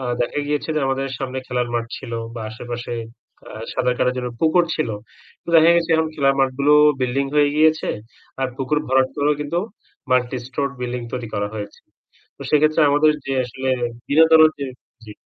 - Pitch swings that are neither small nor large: Yes, average, 3.3 semitones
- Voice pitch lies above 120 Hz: Yes, low, 135 Hz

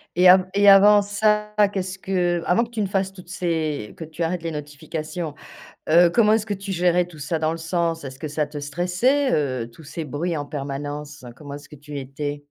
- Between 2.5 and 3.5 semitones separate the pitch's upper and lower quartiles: No, average, 4.4 semitones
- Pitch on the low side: No, medium, 165 Hz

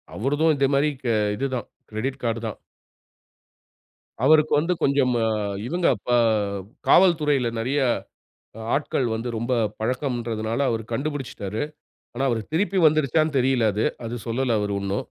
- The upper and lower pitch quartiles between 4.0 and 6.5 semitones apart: Yes, average, 4.3 semitones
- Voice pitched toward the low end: Yes, low, 130 Hz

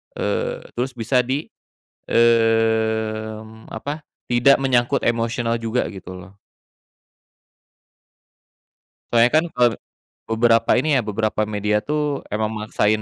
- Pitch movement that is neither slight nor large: No, narrow, 2.2 semitones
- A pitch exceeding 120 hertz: No, low, 115 Hz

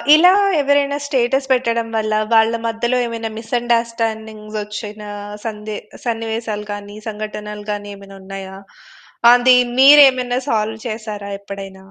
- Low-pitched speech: No, high, 220 Hz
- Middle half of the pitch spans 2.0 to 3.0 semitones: Yes, narrow, 2.4 semitones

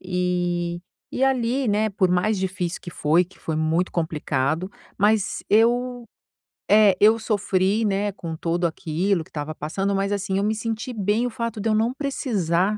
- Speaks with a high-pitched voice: Yes, high, 195 Hz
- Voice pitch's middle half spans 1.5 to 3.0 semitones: No, average, 4.0 semitones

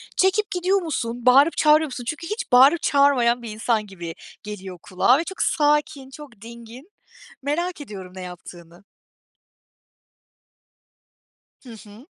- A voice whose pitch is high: Yes, very high, 255 Hz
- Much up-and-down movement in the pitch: Yes, wide, 6.4 semitones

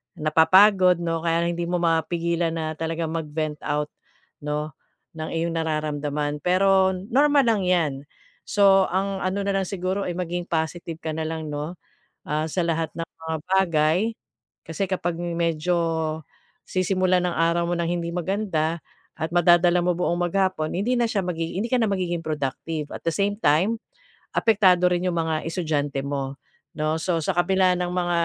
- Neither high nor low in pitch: Yes, medium, 170 Hz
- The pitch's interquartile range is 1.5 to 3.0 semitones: Yes, narrow, 2.6 semitones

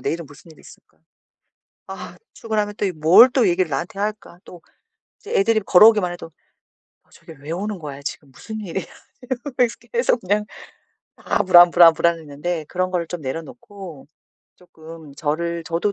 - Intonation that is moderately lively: Yes, average, 4.4 semitones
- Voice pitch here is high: No, medium, 175 Hz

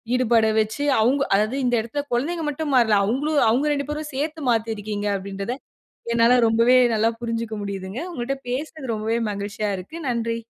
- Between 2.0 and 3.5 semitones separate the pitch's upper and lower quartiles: No, average, 4.2 semitones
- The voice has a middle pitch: No, high, 235 Hz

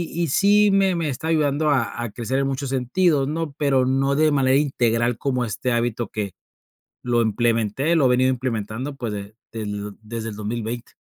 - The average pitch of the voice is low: Yes, low, 130 Hz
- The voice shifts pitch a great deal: No, average, 3.9 semitones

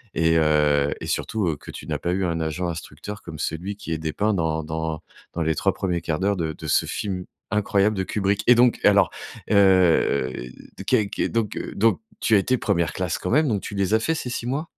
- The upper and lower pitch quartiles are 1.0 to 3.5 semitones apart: No, average, 4.4 semitones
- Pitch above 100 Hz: No, very low, 95 Hz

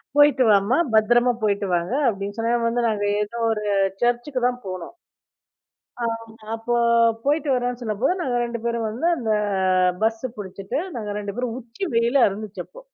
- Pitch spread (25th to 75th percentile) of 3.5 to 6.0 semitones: No, average, 2.8 semitones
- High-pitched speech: Yes, high, 230 Hz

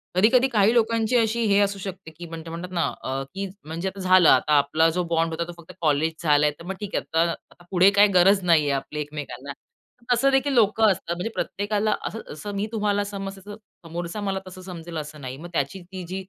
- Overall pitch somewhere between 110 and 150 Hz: No, medium, 185 Hz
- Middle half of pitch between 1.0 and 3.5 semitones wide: No, average, 4.0 semitones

